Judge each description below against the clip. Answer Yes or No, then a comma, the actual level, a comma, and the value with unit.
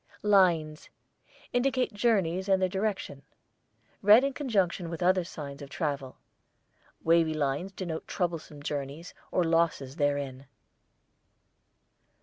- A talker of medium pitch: Yes, medium, 170 Hz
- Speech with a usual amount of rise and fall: Yes, average, 4.8 semitones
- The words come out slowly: Yes, slow, 110 wpm